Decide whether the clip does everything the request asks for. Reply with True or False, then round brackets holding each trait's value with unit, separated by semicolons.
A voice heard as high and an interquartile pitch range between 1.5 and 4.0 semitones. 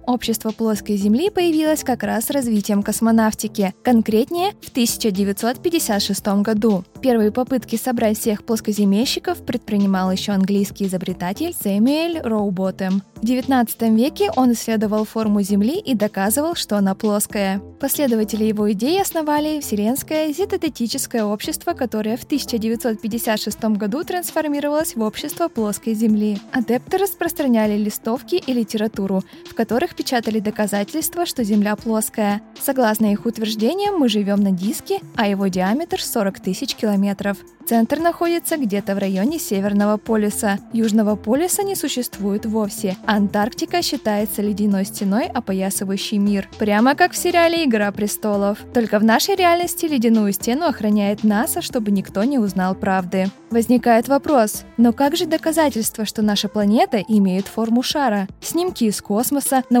False (225 Hz; 5.0 semitones)